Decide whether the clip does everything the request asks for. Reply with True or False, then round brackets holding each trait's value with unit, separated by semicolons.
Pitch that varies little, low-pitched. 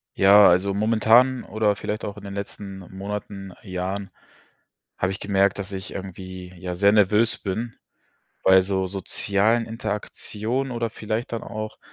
True (2.2 semitones; 100 Hz)